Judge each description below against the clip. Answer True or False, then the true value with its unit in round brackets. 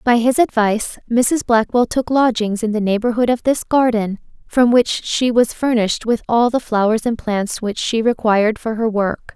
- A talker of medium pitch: False (230 Hz)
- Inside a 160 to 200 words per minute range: True (190 wpm)